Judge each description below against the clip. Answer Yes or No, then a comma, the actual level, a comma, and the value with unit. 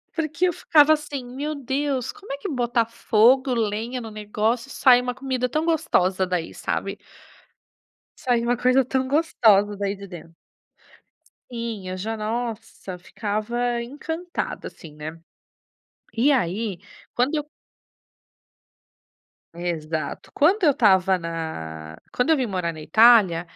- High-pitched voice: Yes, high, 235 Hz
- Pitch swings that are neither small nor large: No, wide, 5.9 semitones